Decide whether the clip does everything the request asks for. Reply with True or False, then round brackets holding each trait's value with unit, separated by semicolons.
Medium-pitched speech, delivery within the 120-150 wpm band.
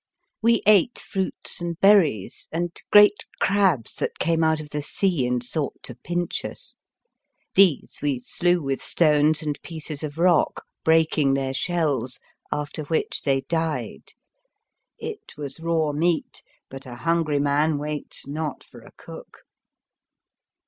True (155 Hz; 140 wpm)